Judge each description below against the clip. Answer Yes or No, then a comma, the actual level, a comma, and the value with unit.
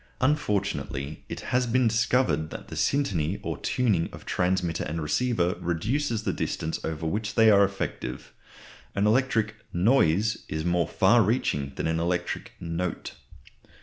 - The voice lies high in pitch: No, very low, 95 Hz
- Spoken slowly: No, average, 145 wpm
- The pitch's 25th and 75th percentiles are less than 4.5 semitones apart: No, wide, 5.6 semitones